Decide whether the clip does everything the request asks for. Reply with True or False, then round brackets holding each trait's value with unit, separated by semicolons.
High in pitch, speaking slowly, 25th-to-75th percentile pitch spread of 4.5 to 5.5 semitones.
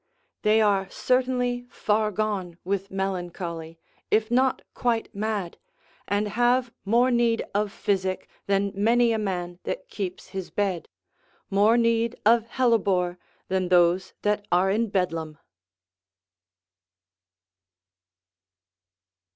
False (205 Hz; 110 wpm; 3.7 semitones)